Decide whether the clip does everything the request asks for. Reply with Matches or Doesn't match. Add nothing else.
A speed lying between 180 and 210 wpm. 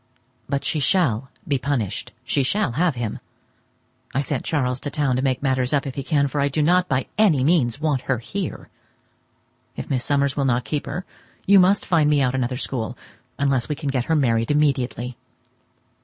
Matches